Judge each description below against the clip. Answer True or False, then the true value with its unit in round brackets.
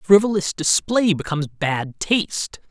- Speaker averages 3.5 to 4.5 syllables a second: True (4.2 syllables/s)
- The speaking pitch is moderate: True (180 Hz)